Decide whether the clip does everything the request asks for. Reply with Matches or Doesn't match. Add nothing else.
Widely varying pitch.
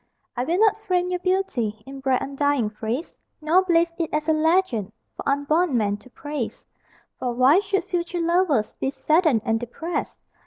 Matches